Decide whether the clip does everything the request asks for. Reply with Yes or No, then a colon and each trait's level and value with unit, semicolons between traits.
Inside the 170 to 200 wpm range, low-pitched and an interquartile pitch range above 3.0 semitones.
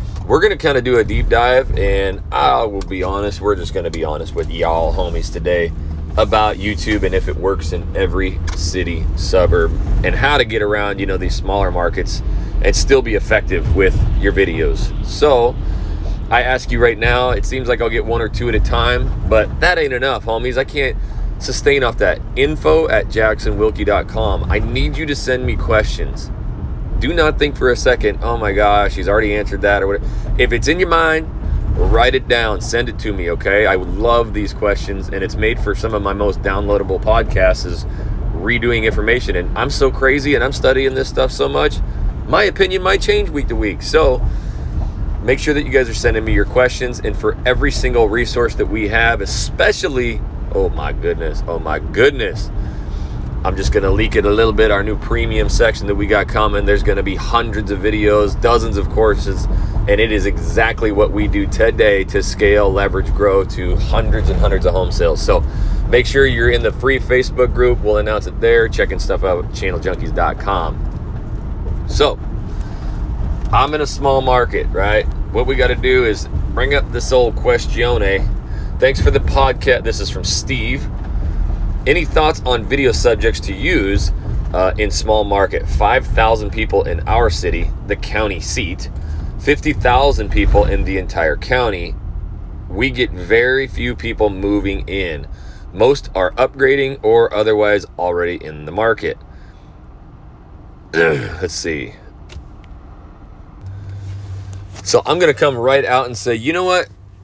Yes: average, 180 wpm; low, 105 Hz; average, 4.0 semitones